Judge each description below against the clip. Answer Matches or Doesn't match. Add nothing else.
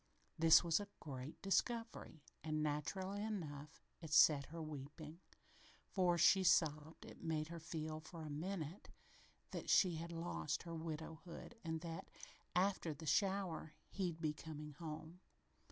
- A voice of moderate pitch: Matches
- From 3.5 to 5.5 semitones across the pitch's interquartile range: Doesn't match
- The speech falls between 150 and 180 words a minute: Doesn't match